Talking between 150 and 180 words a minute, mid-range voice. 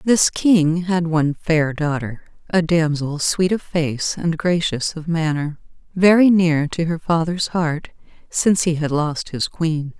Yes: average, 160 wpm; medium, 165 Hz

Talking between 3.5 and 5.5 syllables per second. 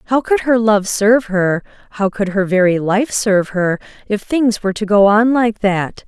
Yes: 4.8 syllables/s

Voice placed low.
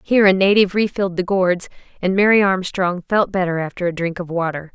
No: medium, 185 Hz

